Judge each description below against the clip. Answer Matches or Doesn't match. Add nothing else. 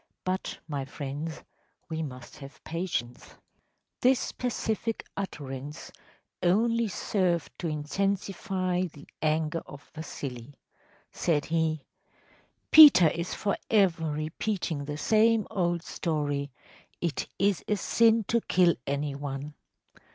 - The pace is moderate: Doesn't match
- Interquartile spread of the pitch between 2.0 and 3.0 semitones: Doesn't match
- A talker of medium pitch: Matches